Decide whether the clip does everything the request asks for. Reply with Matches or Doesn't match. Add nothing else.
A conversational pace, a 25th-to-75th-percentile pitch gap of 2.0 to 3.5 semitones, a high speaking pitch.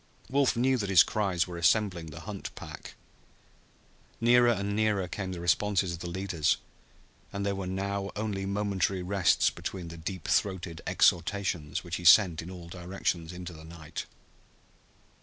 Doesn't match